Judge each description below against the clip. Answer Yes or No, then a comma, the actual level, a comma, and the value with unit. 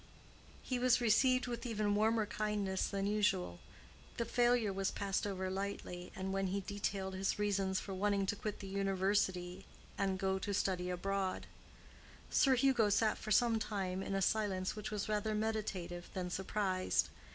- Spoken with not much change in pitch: Yes, narrow, 2.0 semitones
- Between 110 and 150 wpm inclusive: No, average, 165 wpm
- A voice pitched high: Yes, high, 200 Hz